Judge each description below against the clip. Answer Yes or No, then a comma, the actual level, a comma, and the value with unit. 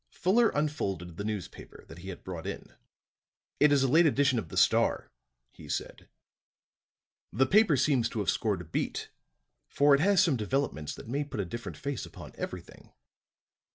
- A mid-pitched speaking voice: No, low, 130 Hz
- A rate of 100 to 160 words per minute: No, average, 175 wpm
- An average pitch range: No, wide, 6.8 semitones